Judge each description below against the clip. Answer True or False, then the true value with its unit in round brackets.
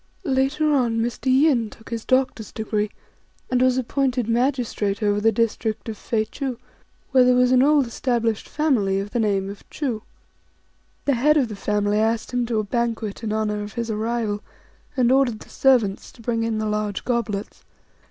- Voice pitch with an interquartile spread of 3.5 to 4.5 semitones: False (3.1 semitones)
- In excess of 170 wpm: True (180 wpm)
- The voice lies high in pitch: True (230 Hz)